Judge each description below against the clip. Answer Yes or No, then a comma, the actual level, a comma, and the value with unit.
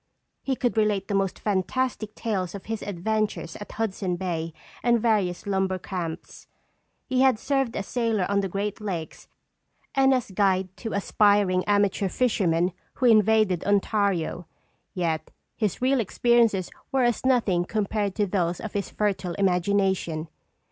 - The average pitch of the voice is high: Yes, high, 200 Hz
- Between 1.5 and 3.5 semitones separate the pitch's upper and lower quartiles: Yes, average, 3.2 semitones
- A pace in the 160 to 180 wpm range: No, average, 145 wpm